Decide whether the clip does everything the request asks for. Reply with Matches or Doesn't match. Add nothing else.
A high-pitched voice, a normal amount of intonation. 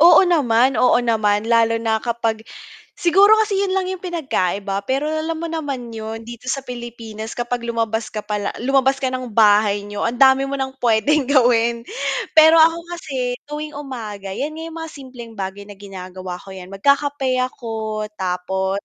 Matches